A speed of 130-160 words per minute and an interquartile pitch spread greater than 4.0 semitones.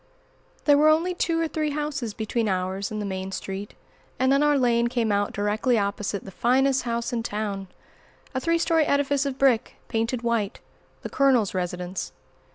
No: average, 175 wpm; wide, 5.5 semitones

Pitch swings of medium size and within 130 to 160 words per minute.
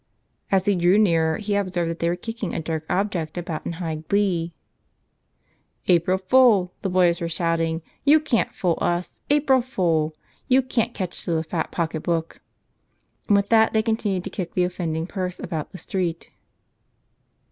No: average, 3.5 semitones; average, 170 wpm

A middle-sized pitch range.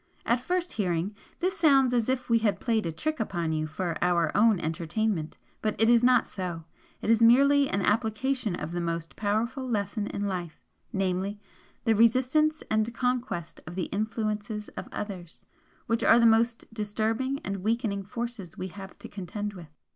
Yes: average, 4.3 semitones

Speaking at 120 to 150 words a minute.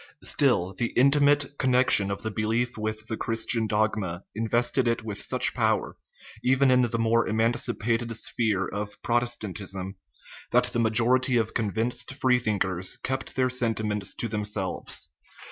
Yes: average, 145 wpm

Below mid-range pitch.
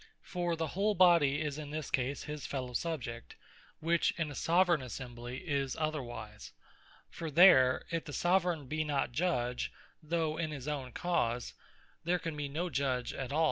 No: medium, 150 Hz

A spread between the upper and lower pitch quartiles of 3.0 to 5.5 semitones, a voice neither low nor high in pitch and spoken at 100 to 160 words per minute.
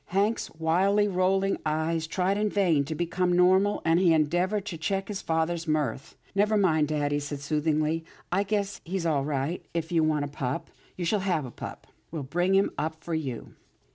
No: average, 3.8 semitones; medium, 165 Hz; average, 200 wpm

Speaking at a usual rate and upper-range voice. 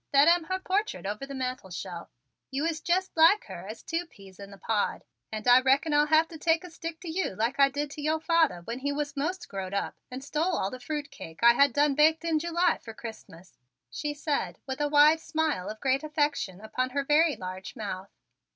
No: fast, 220 wpm; very high, 285 Hz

